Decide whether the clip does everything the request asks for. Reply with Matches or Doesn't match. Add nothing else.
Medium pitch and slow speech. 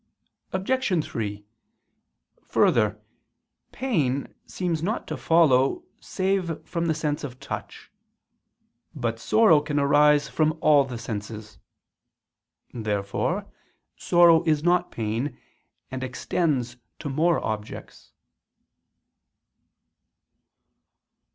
Matches